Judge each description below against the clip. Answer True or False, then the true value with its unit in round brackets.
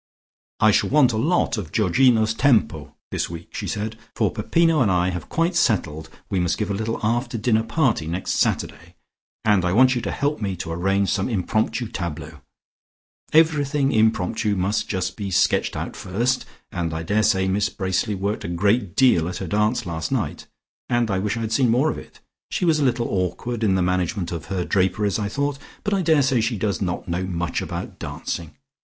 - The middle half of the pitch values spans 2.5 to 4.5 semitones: False (4.9 semitones)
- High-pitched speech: False (105 Hz)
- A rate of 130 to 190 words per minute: False (200 wpm)